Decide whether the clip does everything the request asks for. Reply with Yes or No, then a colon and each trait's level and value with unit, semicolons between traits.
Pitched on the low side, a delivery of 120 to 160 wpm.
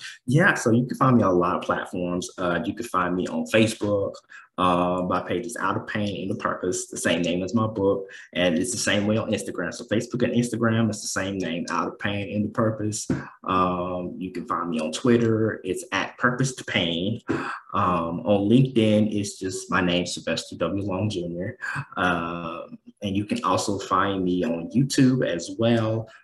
No: low, 100 Hz; fast, 205 wpm